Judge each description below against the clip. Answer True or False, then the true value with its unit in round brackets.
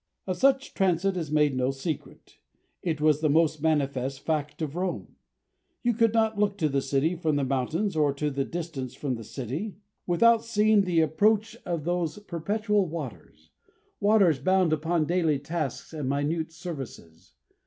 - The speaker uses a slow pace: False (165 wpm)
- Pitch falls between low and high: True (160 Hz)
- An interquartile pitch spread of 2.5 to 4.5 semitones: False (4.9 semitones)